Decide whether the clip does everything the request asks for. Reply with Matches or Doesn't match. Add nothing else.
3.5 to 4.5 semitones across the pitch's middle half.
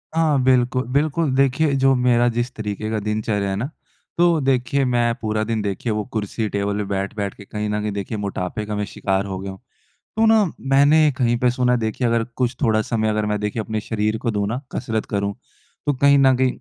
Matches